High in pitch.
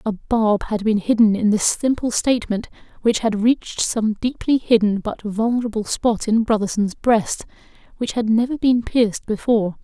Yes: high, 220 Hz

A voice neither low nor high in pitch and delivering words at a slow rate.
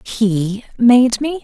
No: high, 235 Hz; slow, 125 wpm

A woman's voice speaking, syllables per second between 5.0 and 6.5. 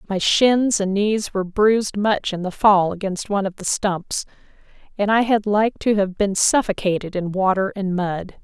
No: female; 4.7 syllables/s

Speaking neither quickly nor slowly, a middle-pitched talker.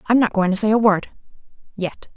No: average, 195 wpm; high, 210 Hz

